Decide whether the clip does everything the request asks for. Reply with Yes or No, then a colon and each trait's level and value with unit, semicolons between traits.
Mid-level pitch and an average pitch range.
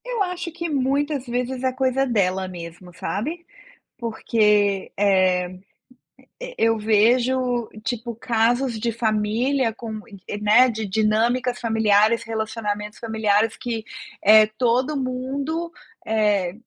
No: high, 230 Hz; average, 3.4 semitones